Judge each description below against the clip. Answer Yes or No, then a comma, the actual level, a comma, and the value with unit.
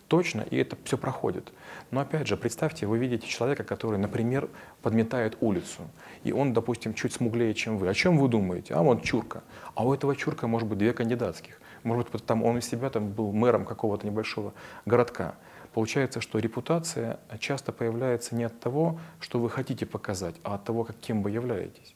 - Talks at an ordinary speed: No, fast, 190 wpm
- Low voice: Yes, low, 115 Hz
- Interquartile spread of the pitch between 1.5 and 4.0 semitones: Yes, average, 2.8 semitones